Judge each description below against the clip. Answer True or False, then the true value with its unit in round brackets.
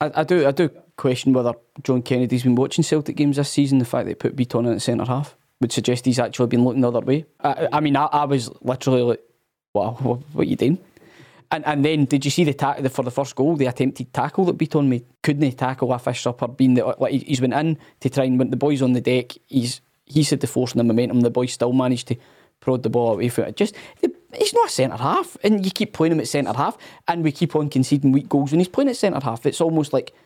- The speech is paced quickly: True (270 wpm)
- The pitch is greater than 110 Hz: True (135 Hz)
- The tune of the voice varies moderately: True (3.3 semitones)